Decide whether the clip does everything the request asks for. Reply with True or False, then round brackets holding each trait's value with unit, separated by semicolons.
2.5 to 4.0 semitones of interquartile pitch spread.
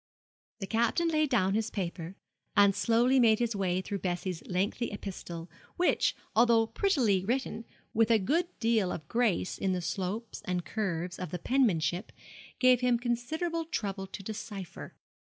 False (4.4 semitones)